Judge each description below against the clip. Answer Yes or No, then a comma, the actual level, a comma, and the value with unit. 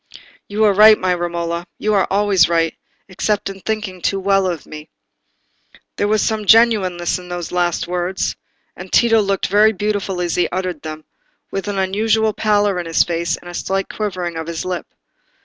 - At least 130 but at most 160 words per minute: No, average, 185 wpm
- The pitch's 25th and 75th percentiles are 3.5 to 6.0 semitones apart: No, average, 3.1 semitones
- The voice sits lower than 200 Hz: Yes, high, 190 Hz